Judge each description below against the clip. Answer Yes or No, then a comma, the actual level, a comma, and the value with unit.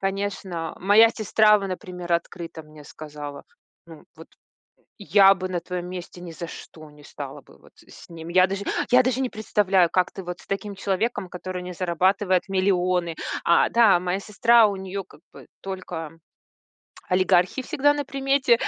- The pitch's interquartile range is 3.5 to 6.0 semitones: No, average, 2.8 semitones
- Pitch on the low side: No, medium, 185 Hz